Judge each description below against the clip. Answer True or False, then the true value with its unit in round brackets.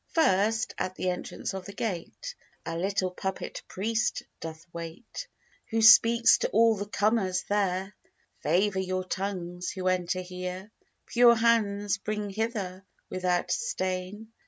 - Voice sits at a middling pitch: False (195 Hz)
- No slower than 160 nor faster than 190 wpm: False (135 wpm)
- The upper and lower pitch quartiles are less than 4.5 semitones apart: True (3.2 semitones)